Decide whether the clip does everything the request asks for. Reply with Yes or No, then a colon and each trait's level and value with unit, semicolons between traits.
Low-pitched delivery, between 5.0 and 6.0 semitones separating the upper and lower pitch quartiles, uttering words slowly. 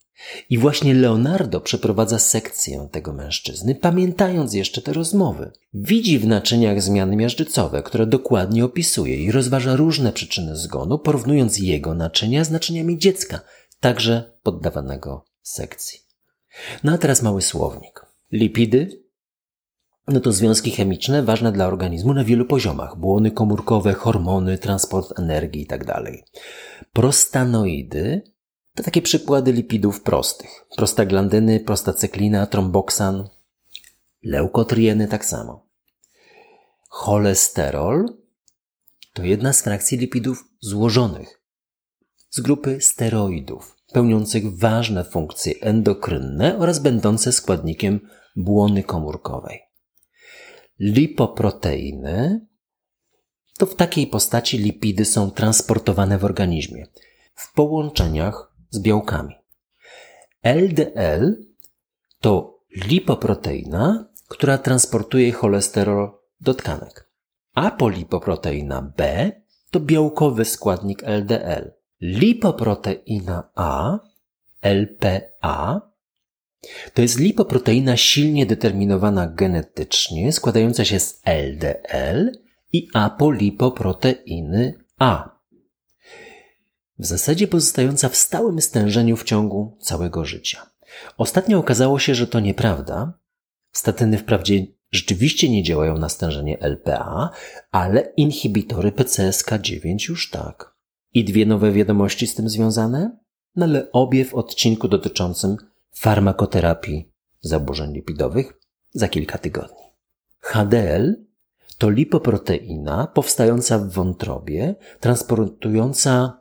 Yes: low, 110 Hz; wide, 5.5 semitones; slow, 95 wpm